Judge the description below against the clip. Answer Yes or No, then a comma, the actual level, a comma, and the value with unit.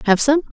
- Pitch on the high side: Yes, very high, 255 Hz